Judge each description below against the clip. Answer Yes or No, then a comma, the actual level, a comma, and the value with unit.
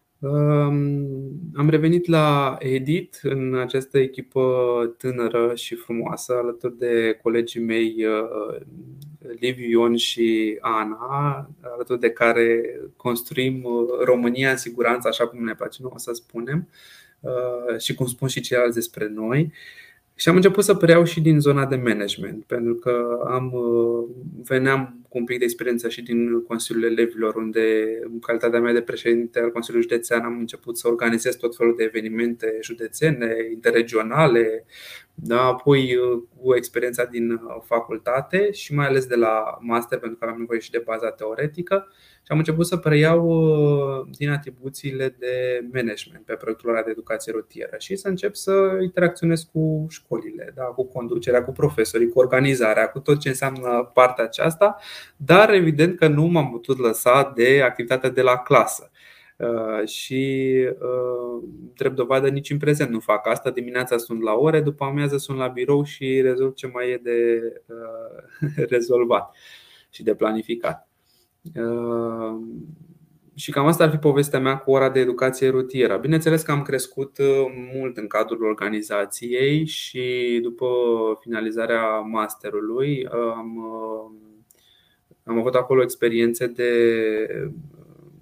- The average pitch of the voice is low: Yes, low, 125 Hz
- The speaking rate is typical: Yes, average, 140 wpm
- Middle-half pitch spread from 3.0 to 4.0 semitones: Yes, average, 3.4 semitones